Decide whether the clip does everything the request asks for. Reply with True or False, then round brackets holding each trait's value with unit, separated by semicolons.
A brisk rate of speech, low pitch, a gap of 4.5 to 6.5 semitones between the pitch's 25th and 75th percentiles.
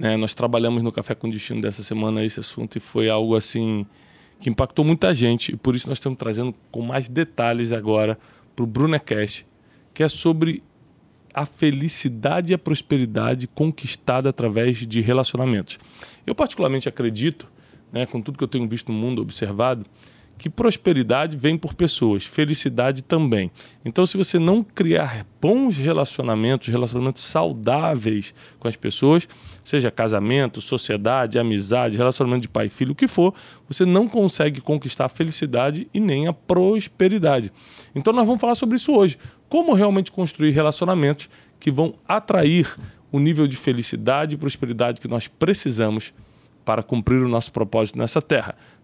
False (155 wpm; 130 Hz; 5.1 semitones)